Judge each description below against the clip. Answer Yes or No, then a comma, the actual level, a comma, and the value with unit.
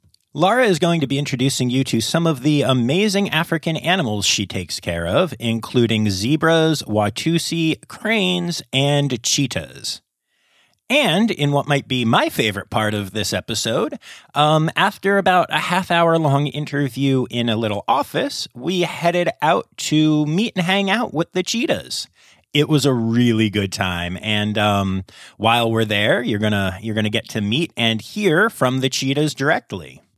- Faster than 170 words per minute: No, average, 165 wpm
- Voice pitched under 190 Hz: Yes, low, 135 Hz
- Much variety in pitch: Yes, wide, 7.0 semitones